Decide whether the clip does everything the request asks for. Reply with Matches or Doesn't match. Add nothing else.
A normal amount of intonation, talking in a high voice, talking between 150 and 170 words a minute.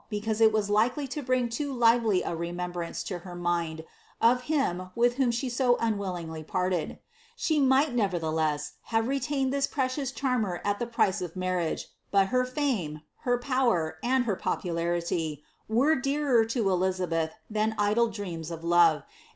Doesn't match